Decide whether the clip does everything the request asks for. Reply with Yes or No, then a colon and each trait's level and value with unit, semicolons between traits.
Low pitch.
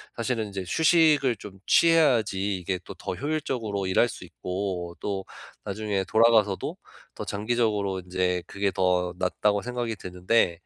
Yes: low, 100 Hz